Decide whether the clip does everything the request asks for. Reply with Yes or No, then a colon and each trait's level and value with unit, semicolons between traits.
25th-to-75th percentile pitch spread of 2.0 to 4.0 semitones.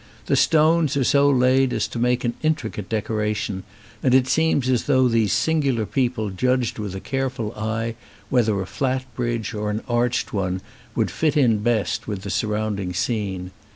Yes: average, 3.6 semitones